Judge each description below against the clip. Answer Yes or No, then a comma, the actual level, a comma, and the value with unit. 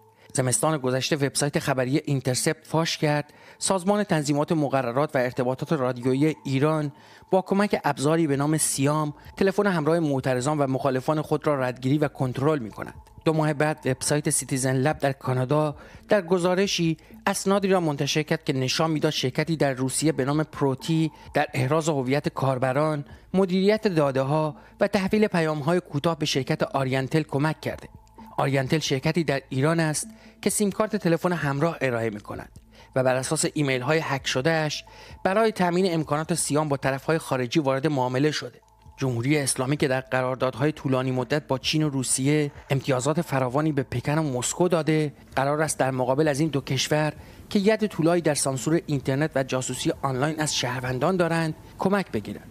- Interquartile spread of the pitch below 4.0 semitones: Yes, average, 3.4 semitones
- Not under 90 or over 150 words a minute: No, average, 160 wpm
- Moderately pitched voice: Yes, medium, 150 Hz